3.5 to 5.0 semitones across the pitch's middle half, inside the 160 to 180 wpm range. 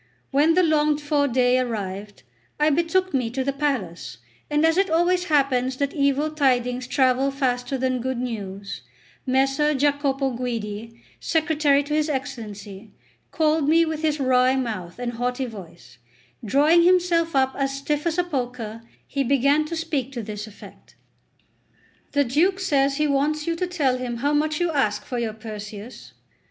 Yes: average, 4.0 semitones; average, 165 wpm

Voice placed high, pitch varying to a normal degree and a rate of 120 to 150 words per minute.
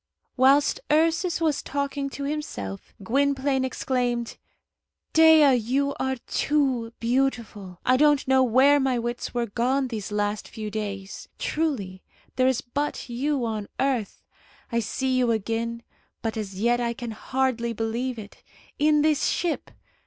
Yes: very high, 255 Hz; average, 3.7 semitones; average, 140 wpm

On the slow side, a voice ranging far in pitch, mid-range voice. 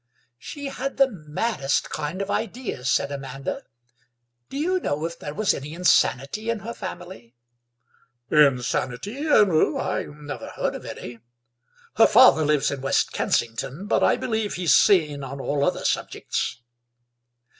No: average, 145 wpm; wide, 7.7 semitones; medium, 155 Hz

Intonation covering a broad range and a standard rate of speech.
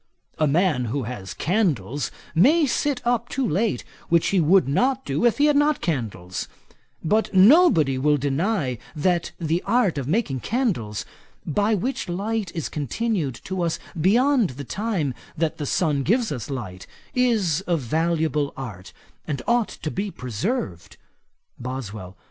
Yes: wide, 8.6 semitones; average, 150 wpm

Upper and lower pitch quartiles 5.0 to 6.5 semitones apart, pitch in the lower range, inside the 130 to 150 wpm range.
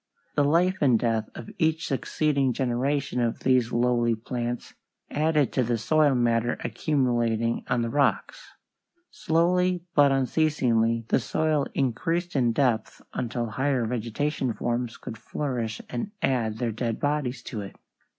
No: average, 3.9 semitones; low, 125 Hz; average, 140 wpm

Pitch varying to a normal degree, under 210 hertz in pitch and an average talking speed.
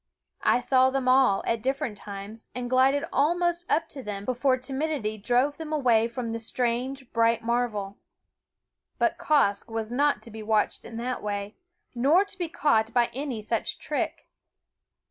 No: average, 3.6 semitones; high, 245 Hz; average, 165 wpm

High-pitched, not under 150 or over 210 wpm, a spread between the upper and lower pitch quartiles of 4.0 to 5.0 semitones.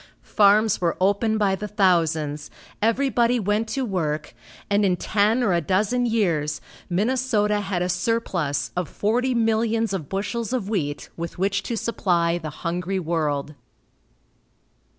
No: high, 200 Hz; average, 140 wpm; average, 4.6 semitones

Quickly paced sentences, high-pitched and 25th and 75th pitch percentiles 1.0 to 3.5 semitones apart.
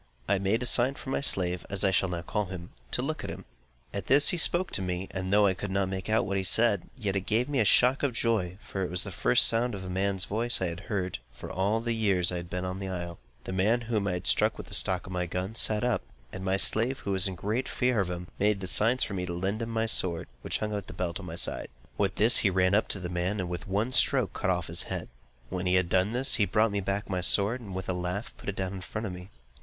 No: fast, 290 wpm; very low, 95 Hz; average, 3.2 semitones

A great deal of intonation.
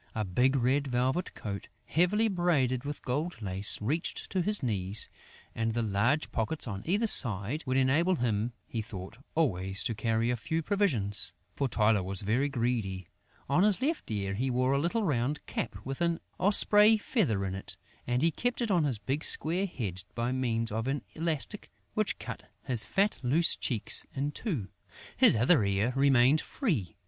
Yes: wide, 6.9 semitones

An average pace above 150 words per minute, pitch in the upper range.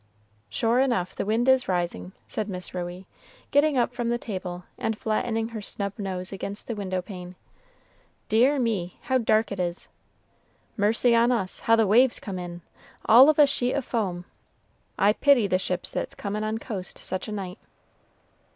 Yes: average, 175 wpm; high, 215 Hz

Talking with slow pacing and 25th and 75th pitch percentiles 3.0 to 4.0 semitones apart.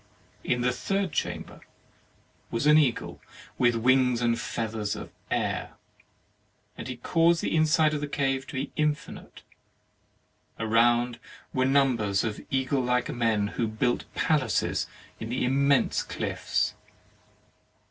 Yes: slow, 125 wpm; average, 3.5 semitones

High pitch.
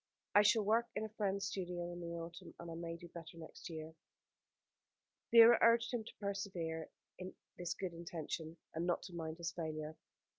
No: medium, 175 Hz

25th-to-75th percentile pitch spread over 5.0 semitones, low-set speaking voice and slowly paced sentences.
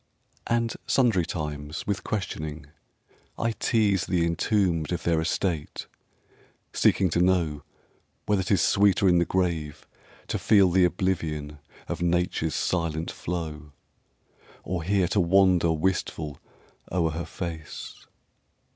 No: average, 3.0 semitones; very low, 85 Hz; slow, 120 wpm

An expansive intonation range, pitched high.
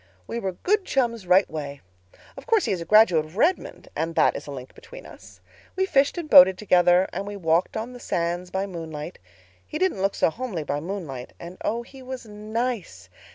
Yes: wide, 6.3 semitones; high, 195 Hz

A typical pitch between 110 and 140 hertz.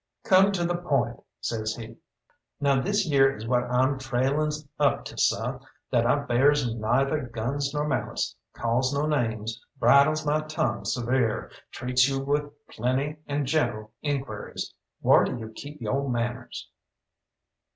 Yes: low, 135 Hz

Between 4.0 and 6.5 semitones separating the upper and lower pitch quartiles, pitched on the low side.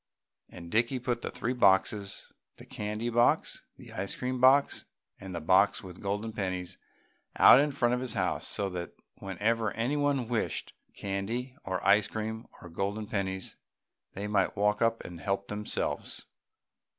No: average, 3.5 semitones; low, 105 Hz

